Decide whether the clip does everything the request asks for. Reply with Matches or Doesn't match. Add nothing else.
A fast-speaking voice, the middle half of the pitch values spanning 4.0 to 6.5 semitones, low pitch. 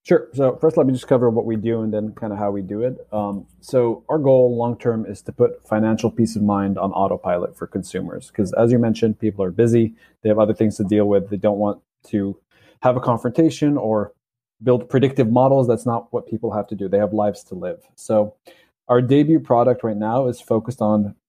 Doesn't match